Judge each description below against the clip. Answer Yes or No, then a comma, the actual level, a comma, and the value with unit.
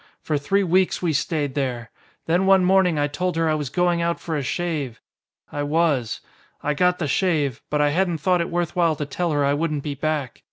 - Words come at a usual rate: No, fast, 220 wpm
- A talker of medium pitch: Yes, medium, 160 Hz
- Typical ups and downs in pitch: Yes, average, 3.4 semitones